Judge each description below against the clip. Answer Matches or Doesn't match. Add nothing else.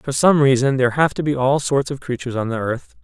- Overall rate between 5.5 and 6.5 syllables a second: Matches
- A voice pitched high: Doesn't match